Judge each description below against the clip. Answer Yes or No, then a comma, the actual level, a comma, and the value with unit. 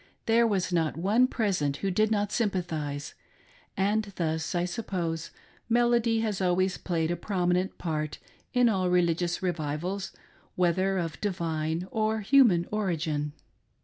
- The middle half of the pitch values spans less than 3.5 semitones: No, average, 4.2 semitones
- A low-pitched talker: No, medium, 180 Hz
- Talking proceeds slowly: Yes, slow, 130 wpm